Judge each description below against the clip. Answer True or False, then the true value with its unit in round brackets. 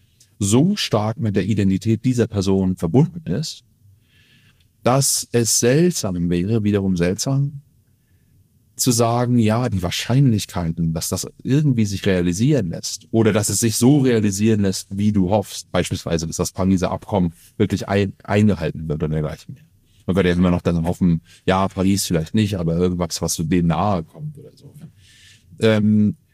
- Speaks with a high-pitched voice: False (105 Hz)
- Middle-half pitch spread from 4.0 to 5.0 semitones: True (4.4 semitones)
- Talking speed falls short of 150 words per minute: False (160 wpm)